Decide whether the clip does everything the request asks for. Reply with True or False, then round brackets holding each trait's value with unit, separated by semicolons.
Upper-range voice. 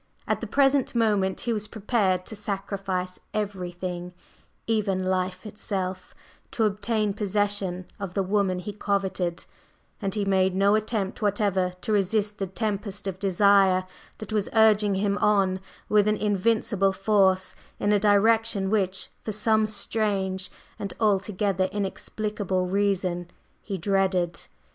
True (200 Hz)